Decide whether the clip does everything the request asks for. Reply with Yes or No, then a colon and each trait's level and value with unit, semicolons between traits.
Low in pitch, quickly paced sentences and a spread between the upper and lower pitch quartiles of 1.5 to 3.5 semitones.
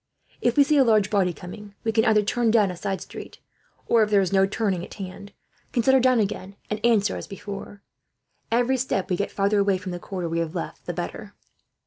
No: high, 205 Hz; fast, 235 wpm; average, 2.9 semitones